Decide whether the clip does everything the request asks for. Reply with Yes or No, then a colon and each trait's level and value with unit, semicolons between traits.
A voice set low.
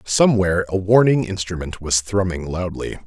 Yes: very low, 95 Hz